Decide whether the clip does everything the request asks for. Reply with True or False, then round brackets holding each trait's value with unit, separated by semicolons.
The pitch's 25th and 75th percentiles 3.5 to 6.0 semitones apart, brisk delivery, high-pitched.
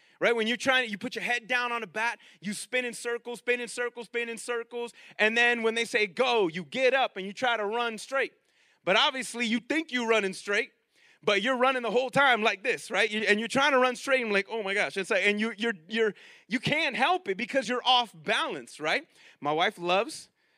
False (2.9 semitones; 250 wpm; 235 Hz)